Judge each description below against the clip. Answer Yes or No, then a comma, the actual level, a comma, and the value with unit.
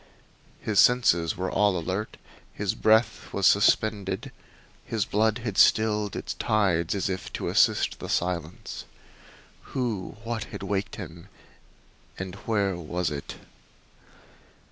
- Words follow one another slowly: Yes, slow, 120 wpm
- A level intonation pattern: No, average, 3.2 semitones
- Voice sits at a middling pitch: No, low, 100 Hz